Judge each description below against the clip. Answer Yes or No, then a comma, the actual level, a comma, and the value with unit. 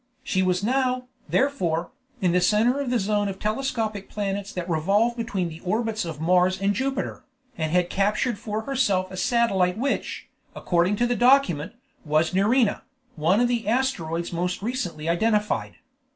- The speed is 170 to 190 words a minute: No, average, 160 wpm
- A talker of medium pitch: No, high, 205 Hz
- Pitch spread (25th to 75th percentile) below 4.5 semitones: No, average, 4.8 semitones